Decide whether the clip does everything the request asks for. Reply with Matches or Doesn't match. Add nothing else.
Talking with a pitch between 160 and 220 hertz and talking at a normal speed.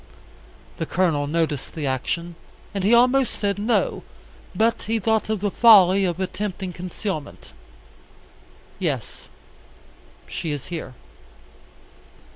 Doesn't match